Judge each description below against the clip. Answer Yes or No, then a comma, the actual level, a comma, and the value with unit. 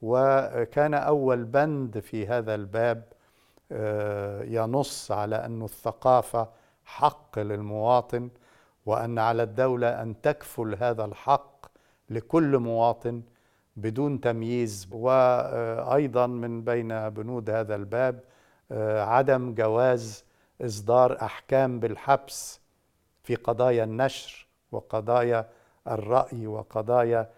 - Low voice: Yes, low, 120 Hz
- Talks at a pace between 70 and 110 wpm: Yes, average, 90 wpm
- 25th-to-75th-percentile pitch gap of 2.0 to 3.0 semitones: Yes, narrow, 2.5 semitones